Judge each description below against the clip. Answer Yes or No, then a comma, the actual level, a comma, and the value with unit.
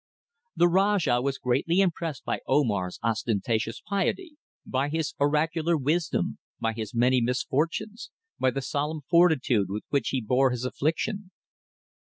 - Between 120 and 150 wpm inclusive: Yes, slow, 135 wpm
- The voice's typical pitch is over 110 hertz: Yes, medium, 140 Hz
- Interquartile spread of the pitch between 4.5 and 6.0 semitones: Yes, average, 5.3 semitones